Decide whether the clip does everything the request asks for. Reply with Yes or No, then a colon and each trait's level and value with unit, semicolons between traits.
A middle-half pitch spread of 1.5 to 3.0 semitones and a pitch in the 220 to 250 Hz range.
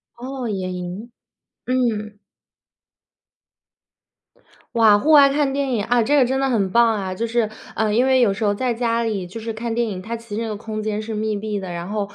Yes: average, 2.7 semitones; high, 225 Hz